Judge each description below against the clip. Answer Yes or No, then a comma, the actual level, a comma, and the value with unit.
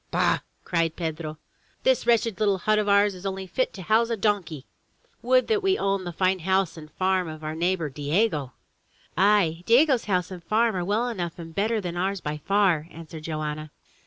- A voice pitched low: No, medium, 185 Hz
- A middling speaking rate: Yes, average, 190 wpm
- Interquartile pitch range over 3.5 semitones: Yes, average, 4.5 semitones